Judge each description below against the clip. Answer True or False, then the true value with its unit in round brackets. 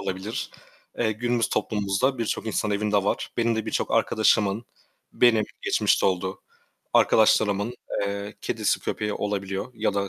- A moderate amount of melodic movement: False (2.0 semitones)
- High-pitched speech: False (105 Hz)